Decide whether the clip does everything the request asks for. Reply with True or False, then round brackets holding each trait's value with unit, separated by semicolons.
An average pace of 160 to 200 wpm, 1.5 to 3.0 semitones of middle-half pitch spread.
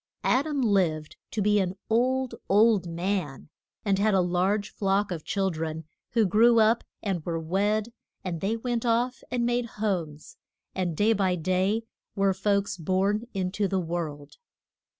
False (165 wpm; 3.7 semitones)